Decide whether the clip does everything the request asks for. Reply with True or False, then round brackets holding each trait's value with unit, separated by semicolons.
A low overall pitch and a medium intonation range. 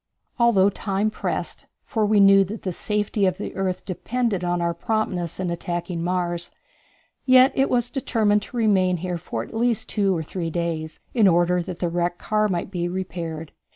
False (185 Hz; 3.6 semitones)